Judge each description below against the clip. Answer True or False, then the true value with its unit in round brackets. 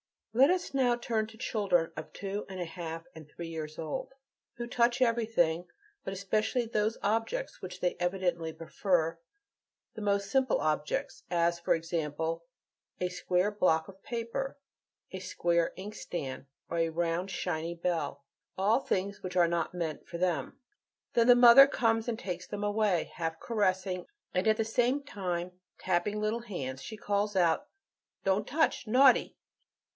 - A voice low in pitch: False (190 Hz)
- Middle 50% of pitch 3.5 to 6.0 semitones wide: True (4.8 semitones)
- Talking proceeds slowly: False (160 wpm)